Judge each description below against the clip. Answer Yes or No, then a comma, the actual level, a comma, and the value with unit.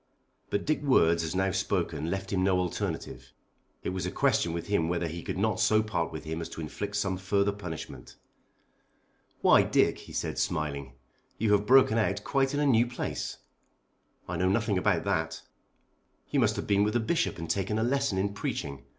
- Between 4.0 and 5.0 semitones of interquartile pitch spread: Yes, average, 4.3 semitones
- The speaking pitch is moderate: No, very low, 95 Hz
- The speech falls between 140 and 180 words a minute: No, average, 195 wpm